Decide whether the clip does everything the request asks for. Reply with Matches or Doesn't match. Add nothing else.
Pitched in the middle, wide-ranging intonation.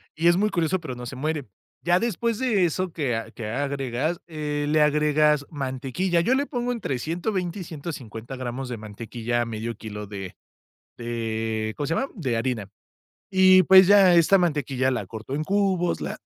Matches